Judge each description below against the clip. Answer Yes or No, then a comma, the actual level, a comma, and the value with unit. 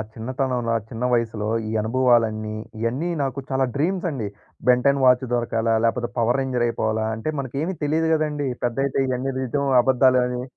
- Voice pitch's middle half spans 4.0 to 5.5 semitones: No, average, 2.9 semitones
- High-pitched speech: No, low, 125 Hz